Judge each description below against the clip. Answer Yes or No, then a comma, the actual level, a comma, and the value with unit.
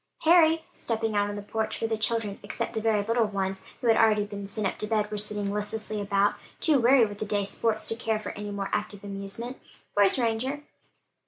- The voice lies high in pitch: Yes, high, 215 Hz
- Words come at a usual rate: No, fast, 215 wpm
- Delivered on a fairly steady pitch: Yes, narrow, 1.8 semitones